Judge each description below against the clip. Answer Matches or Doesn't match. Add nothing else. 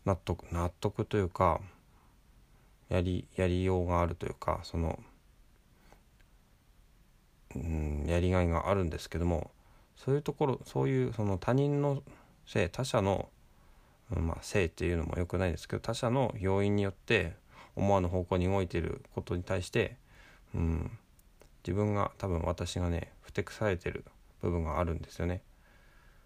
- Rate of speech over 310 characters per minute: Doesn't match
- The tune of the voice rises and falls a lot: Doesn't match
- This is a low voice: Matches